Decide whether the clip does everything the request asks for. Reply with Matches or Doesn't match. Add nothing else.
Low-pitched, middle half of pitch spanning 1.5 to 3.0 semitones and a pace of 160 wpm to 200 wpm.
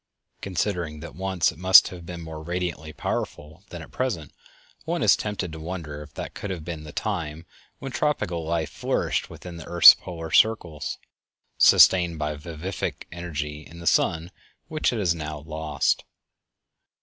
Matches